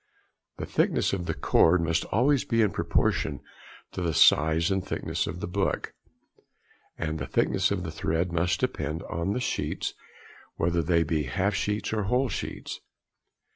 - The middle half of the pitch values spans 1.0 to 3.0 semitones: No, average, 3.6 semitones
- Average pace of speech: Yes, average, 165 wpm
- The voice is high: No, very low, 90 Hz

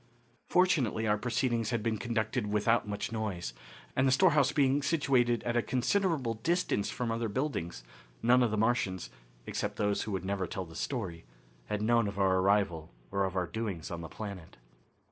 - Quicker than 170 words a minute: Yes, average, 180 wpm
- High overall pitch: No, low, 110 Hz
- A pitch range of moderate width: Yes, average, 4.1 semitones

